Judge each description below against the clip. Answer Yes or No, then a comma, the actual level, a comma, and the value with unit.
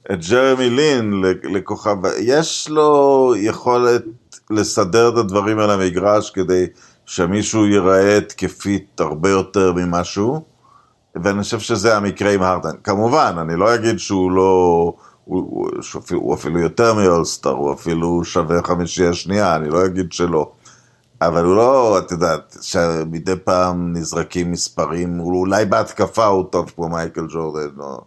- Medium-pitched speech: No, very low, 95 Hz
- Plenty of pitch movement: No, average, 3.6 semitones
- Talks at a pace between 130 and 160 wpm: Yes, average, 140 wpm